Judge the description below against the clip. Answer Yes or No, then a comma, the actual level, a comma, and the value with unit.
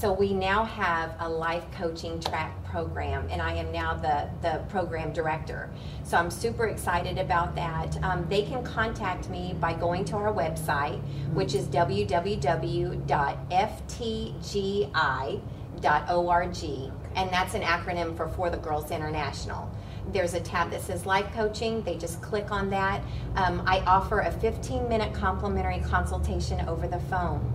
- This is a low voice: No, medium, 145 Hz